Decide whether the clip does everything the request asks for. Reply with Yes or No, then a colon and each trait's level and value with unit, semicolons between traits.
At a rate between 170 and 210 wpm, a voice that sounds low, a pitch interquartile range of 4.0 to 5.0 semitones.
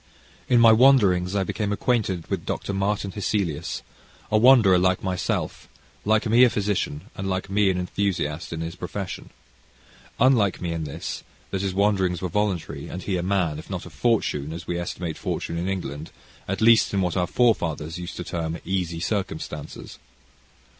No: average, 175 wpm; very low, 95 Hz; average, 3.4 semitones